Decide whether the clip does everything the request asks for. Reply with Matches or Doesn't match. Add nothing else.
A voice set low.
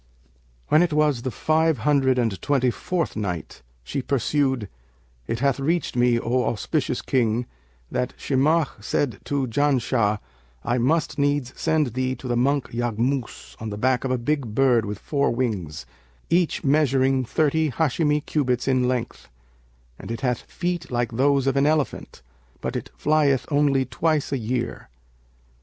Matches